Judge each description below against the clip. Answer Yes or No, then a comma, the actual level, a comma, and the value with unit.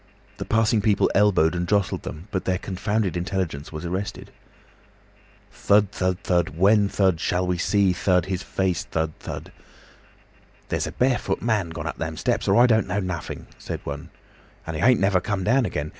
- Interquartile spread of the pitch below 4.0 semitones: Yes, average, 2.7 semitones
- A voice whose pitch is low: Yes, very low, 95 Hz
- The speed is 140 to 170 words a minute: No, average, 180 wpm